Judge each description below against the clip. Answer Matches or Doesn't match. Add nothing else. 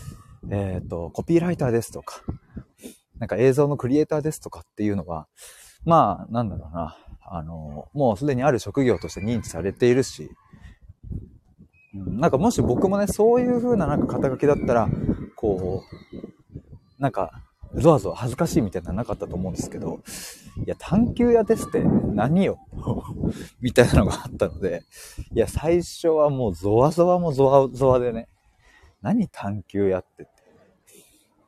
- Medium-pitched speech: Doesn't match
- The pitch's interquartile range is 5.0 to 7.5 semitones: Doesn't match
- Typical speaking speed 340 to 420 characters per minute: Doesn't match